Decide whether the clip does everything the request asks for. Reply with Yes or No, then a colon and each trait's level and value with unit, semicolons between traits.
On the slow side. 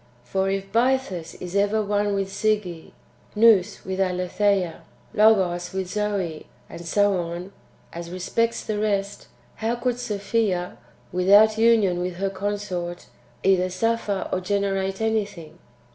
Yes: slow, 130 wpm